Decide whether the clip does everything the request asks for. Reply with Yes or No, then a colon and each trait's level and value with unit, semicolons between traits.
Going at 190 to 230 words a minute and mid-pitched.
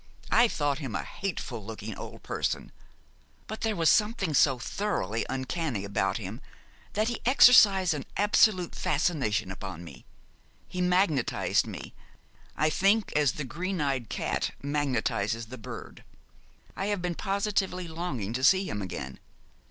No: average, 145 wpm; medium, 150 Hz